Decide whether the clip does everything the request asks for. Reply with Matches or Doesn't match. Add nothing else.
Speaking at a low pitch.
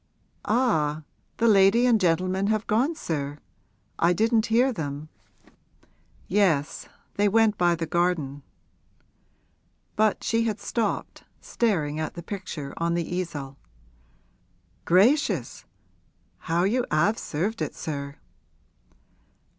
Doesn't match